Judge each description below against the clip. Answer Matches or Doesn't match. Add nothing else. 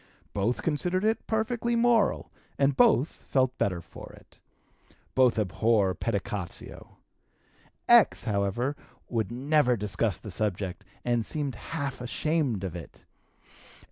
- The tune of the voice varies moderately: Doesn't match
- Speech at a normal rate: Doesn't match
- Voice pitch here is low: Matches